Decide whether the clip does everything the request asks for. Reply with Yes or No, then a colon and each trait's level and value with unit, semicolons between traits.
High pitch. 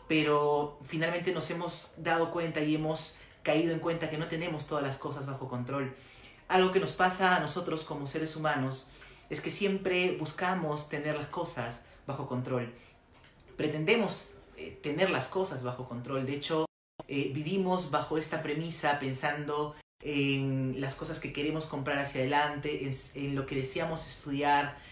No: medium, 150 Hz